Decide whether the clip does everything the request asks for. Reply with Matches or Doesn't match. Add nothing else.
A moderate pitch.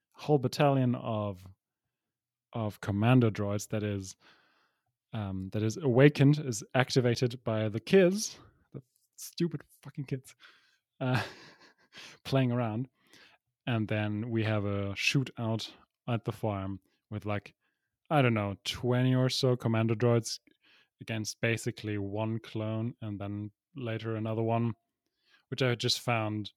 Doesn't match